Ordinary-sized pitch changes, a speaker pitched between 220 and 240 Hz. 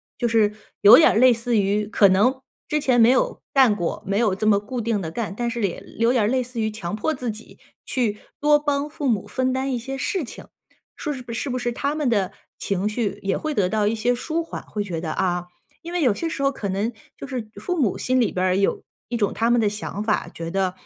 Yes: average, 4.2 semitones; high, 230 Hz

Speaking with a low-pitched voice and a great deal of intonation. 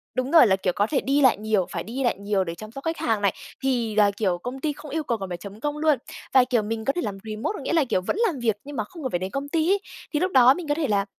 No: high, 240 Hz; wide, 6.0 semitones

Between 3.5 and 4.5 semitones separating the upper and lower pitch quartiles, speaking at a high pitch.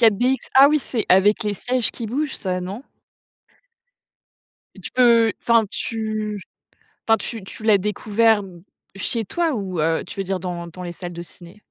Yes: average, 3.8 semitones; high, 210 Hz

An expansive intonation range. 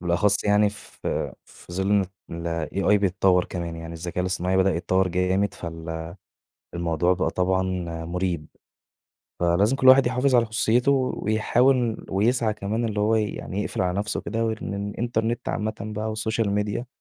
No: average, 3.6 semitones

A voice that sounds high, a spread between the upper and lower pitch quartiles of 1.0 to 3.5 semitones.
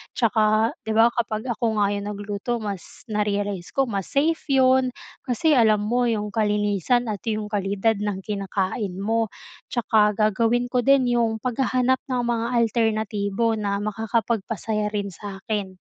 Yes: high, 220 Hz; narrow, 2.6 semitones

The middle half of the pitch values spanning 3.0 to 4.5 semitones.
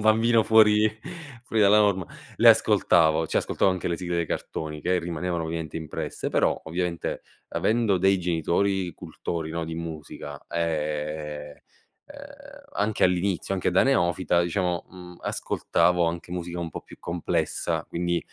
No: narrow, 2.6 semitones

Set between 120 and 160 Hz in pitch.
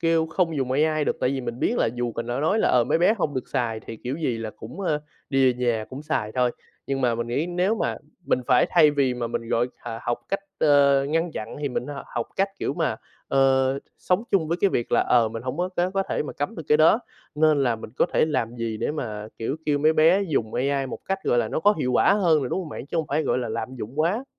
Yes: medium, 140 Hz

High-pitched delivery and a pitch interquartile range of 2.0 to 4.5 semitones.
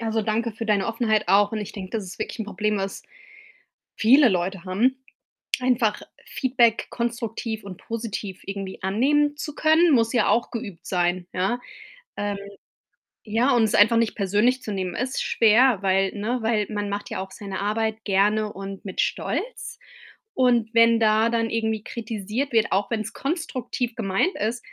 Yes: high, 220 Hz; average, 2.9 semitones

